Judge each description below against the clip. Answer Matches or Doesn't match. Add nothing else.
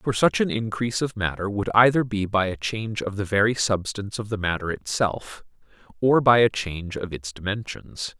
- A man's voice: Matches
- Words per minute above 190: Matches